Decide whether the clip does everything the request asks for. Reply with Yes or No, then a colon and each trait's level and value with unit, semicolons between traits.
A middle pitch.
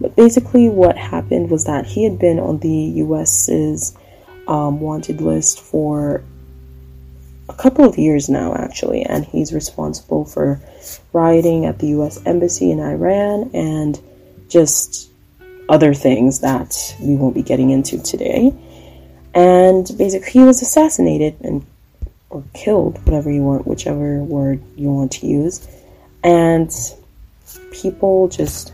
Yes: medium, 145 Hz